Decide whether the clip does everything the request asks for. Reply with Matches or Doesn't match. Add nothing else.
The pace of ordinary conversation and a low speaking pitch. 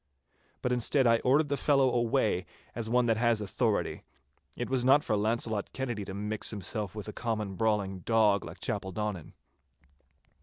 Matches